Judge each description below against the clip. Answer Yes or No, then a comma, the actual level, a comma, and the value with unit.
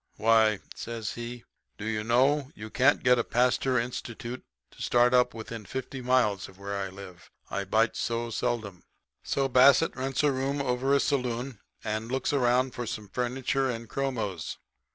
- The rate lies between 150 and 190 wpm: Yes, average, 170 wpm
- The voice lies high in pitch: No, low, 120 Hz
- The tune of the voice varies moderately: Yes, average, 3.0 semitones